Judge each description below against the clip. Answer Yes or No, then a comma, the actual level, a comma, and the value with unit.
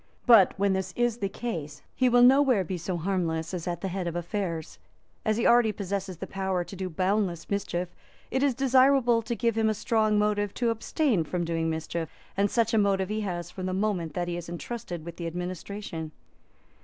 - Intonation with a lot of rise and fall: No, average, 4.3 semitones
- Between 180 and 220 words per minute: Yes, fast, 205 wpm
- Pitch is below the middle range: No, high, 195 Hz